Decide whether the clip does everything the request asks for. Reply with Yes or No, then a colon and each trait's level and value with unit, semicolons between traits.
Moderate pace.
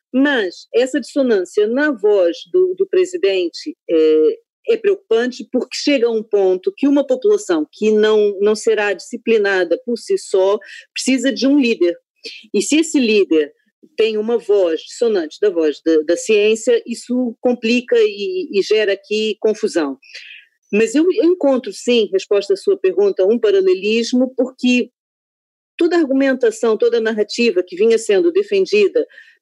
Yes: average, 145 wpm